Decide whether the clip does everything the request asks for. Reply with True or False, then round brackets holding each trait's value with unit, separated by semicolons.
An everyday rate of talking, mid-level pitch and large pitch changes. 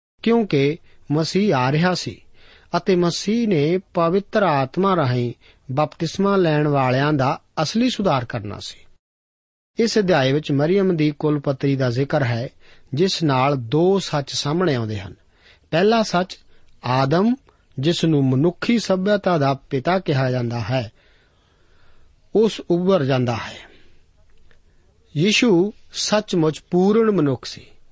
True (125 wpm; 150 Hz; 7.1 semitones)